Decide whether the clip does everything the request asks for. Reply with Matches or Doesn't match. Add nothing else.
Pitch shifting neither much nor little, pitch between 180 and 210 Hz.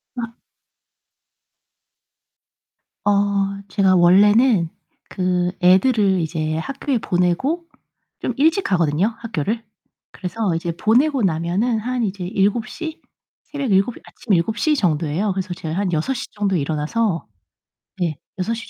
Matches